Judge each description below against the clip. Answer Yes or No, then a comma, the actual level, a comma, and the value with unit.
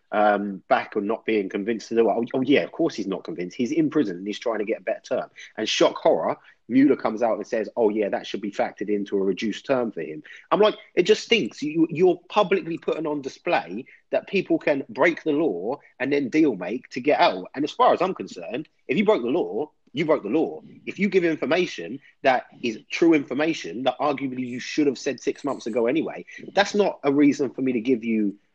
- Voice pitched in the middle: Yes, medium, 145 Hz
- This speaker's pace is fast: Yes, fast, 240 wpm